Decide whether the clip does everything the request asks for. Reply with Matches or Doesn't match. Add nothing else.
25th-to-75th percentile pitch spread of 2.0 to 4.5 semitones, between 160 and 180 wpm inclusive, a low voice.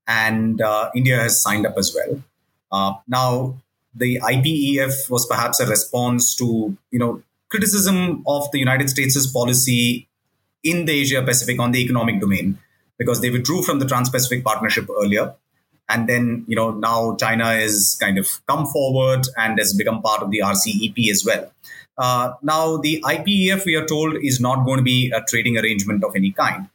Matches